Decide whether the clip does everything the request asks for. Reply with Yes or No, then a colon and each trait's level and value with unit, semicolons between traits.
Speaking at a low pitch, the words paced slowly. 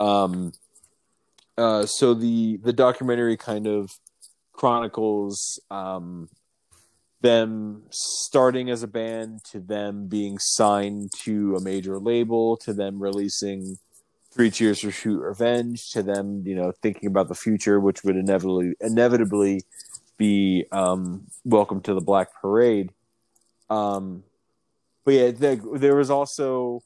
Yes: low, 105 Hz; slow, 125 wpm